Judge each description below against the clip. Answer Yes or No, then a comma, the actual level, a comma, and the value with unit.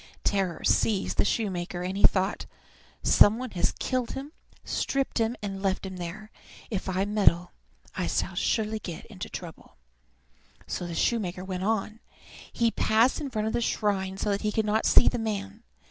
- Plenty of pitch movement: No, average, 2.8 semitones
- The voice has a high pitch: Yes, high, 205 Hz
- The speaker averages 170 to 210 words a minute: Yes, average, 175 wpm